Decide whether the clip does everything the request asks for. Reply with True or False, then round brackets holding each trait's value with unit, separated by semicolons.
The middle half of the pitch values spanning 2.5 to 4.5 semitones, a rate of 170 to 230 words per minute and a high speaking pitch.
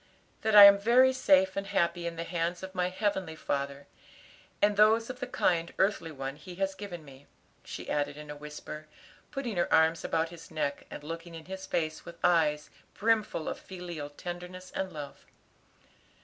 False (3.9 semitones; 180 wpm; 175 Hz)